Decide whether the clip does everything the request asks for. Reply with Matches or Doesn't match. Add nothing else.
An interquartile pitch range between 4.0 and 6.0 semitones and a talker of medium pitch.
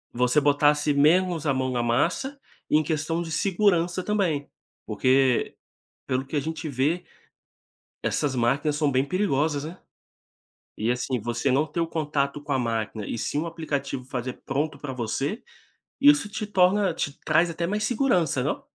Matches